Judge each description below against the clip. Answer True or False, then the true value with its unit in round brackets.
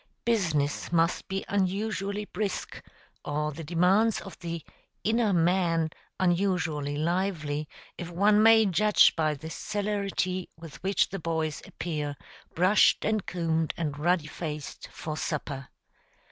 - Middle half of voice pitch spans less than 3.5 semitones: False (4.0 semitones)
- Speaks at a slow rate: True (125 wpm)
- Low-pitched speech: False (175 Hz)